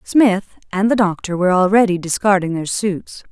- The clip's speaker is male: No, female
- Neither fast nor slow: Yes, average, 165 wpm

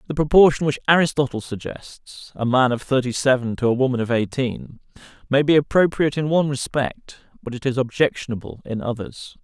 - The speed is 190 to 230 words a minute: No, average, 170 wpm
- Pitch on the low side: Yes, low, 130 Hz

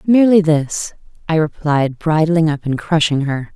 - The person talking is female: Yes, female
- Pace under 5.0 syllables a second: Yes, 4.5 syllables/s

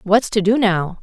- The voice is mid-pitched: No, high, 205 Hz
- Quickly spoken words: Yes, fast, 235 wpm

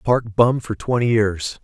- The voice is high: No, low, 110 Hz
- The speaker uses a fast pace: No, average, 185 wpm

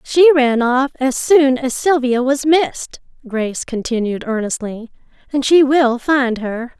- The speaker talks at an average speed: Yes, average, 150 wpm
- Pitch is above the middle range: Yes, very high, 260 Hz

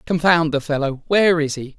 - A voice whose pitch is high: No, medium, 155 Hz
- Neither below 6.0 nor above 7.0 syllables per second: No, 5.6 syllables/s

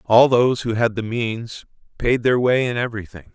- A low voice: Yes, low, 115 Hz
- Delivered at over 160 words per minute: Yes, average, 200 wpm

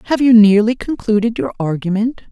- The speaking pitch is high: Yes, high, 215 Hz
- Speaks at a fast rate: No, average, 155 wpm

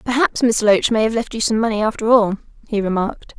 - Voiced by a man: No, female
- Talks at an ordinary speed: No, fast, 230 wpm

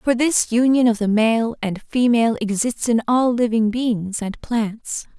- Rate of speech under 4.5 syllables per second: Yes, 4.1 syllables/s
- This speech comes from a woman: Yes, female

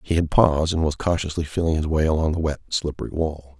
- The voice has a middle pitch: No, very low, 80 Hz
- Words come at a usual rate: No, fast, 235 wpm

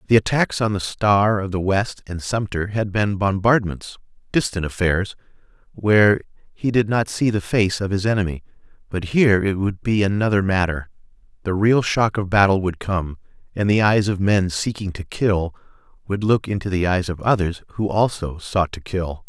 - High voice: No, low, 100 Hz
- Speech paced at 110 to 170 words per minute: No, average, 185 wpm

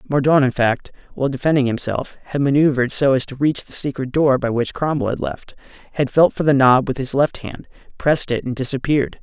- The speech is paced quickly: Yes, fast, 215 wpm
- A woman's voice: No, male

